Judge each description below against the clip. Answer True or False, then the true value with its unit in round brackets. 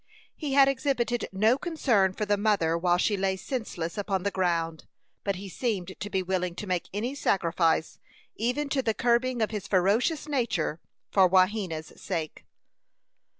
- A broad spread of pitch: False (4.7 semitones)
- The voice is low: False (200 Hz)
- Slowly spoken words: False (160 wpm)